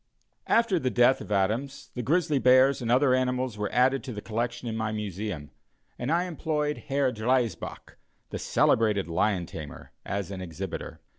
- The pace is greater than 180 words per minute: No, average, 165 wpm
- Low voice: Yes, low, 120 Hz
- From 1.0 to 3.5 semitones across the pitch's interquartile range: No, average, 4.4 semitones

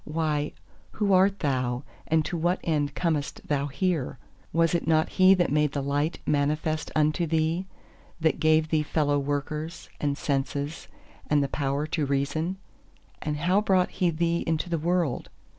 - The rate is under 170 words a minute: Yes, average, 160 wpm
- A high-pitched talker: No, medium, 155 Hz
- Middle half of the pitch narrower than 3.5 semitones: Yes, average, 2.7 semitones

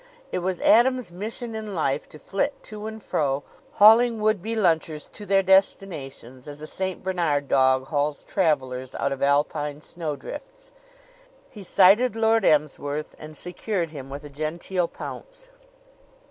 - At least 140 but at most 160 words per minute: Yes, average, 145 wpm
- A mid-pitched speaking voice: Yes, medium, 175 Hz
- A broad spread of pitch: Yes, wide, 6.7 semitones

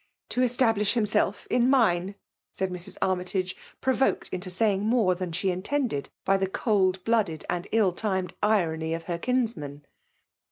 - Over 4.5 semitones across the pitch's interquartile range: No, average, 3.8 semitones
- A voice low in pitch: No, high, 190 Hz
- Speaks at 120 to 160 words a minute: Yes, average, 155 wpm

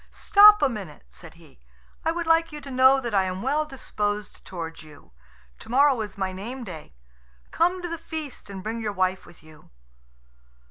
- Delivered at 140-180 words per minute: No, average, 190 wpm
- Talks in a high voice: Yes, high, 225 Hz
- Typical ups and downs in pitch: No, wide, 8.1 semitones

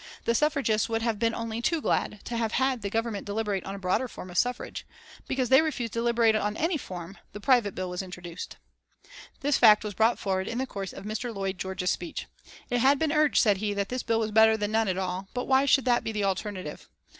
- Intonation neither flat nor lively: Yes, average, 3.8 semitones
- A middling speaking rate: No, fast, 235 wpm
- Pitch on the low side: No, high, 220 Hz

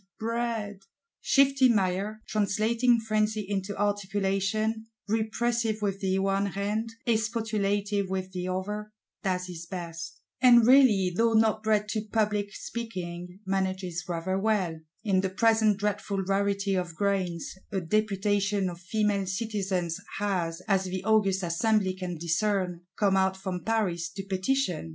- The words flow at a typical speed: No, slow, 130 wpm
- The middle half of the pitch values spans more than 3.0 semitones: No, narrow, 2.5 semitones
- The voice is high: Yes, high, 200 Hz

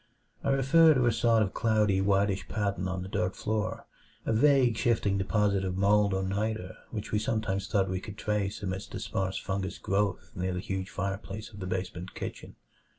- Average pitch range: No, narrow, 2.3 semitones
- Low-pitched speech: Yes, low, 100 Hz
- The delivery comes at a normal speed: Yes, average, 190 wpm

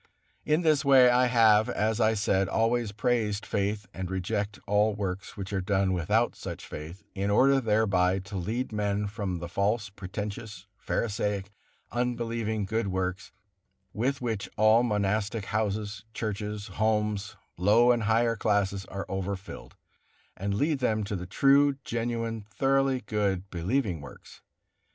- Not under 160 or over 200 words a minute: No, average, 140 wpm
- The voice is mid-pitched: No, low, 105 Hz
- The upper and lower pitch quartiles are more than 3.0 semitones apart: No, average, 2.7 semitones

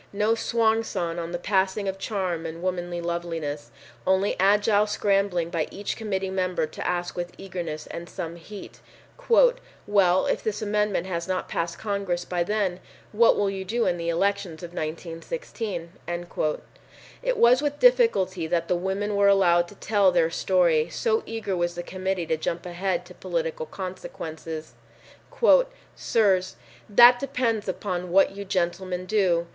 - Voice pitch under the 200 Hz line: Yes, medium, 185 Hz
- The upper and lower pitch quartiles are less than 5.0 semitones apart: Yes, average, 3.1 semitones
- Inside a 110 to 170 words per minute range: Yes, average, 155 wpm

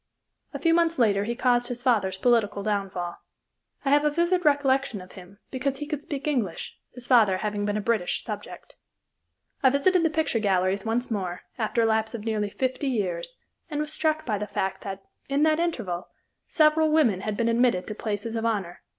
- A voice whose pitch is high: Yes, high, 230 Hz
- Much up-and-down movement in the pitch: Yes, wide, 5.9 semitones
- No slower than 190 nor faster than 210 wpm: Yes, average, 195 wpm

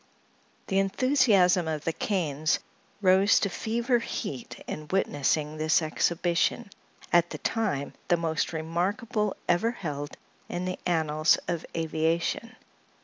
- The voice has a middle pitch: Yes, medium, 175 Hz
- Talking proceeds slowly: Yes, slow, 120 wpm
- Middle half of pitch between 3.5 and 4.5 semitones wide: Yes, average, 4.1 semitones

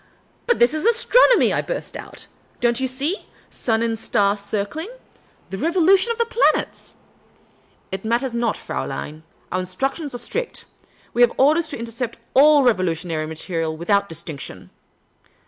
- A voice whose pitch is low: No, high, 235 Hz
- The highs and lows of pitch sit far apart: Yes, wide, 8.2 semitones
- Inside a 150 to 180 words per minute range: Yes, average, 160 wpm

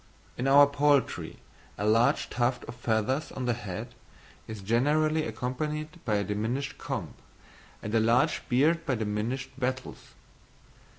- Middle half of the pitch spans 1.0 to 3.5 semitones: No, average, 4.3 semitones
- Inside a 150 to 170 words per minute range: No, slow, 135 wpm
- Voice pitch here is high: No, low, 125 Hz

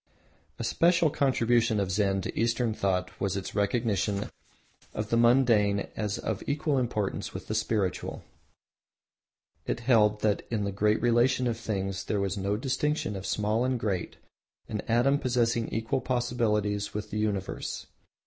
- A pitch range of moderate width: Yes, average, 3.0 semitones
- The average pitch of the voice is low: Yes, low, 110 Hz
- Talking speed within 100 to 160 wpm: Yes, average, 150 wpm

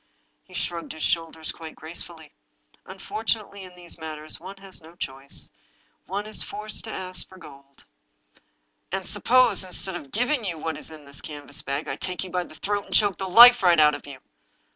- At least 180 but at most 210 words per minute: Yes, average, 200 wpm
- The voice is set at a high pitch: No, medium, 175 Hz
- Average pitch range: Yes, average, 4.2 semitones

